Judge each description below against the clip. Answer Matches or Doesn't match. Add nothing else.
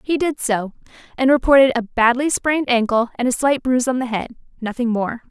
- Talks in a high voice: Matches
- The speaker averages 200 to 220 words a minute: Matches